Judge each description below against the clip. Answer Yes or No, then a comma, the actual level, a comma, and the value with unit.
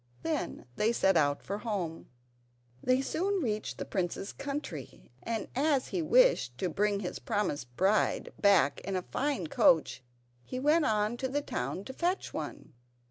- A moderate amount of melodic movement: No, wide, 7.9 semitones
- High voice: Yes, high, 210 Hz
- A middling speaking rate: Yes, average, 160 wpm